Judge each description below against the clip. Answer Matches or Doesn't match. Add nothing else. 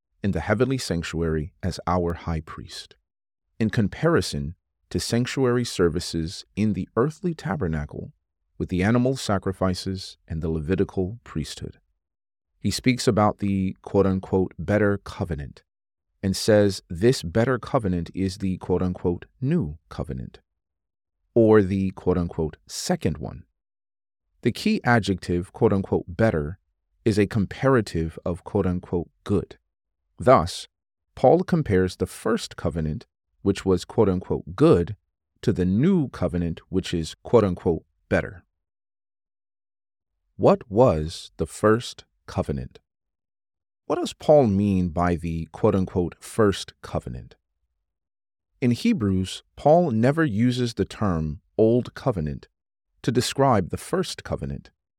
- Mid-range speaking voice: Doesn't match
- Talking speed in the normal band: Doesn't match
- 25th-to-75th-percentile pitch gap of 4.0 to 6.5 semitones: Matches